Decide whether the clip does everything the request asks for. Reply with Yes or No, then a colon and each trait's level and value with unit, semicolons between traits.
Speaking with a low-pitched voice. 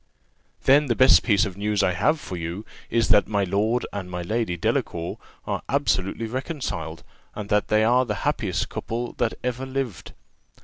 Yes: low, 105 Hz